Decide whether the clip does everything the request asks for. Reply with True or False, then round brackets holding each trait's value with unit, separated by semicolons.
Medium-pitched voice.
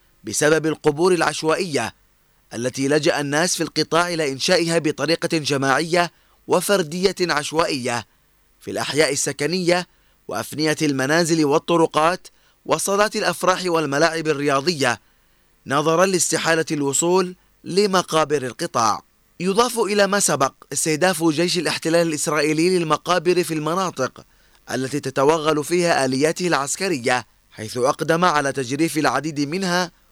True (160 Hz)